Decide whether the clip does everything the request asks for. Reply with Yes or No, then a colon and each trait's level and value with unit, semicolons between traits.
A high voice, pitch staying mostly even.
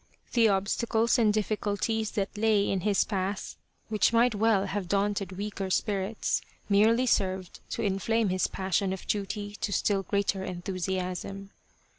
Yes: high, 200 Hz; narrow, 2.1 semitones